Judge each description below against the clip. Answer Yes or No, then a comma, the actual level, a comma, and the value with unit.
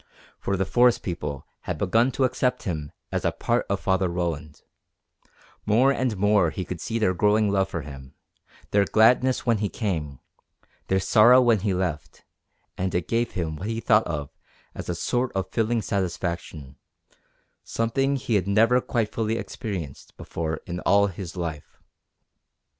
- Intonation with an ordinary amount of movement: Yes, average, 4.9 semitones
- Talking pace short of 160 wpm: No, average, 165 wpm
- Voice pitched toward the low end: Yes, low, 100 Hz